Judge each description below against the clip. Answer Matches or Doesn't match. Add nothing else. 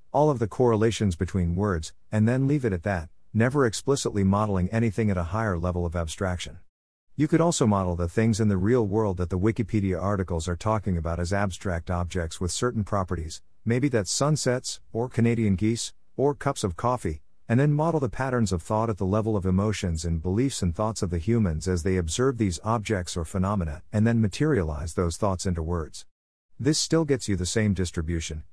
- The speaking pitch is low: Matches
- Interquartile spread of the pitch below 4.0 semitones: Doesn't match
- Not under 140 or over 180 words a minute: Doesn't match